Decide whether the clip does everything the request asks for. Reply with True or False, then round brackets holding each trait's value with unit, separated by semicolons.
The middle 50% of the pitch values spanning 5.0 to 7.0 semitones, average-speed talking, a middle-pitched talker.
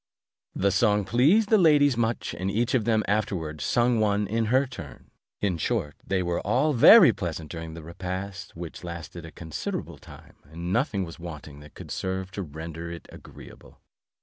False (5.6 semitones; 175 wpm; 95 Hz)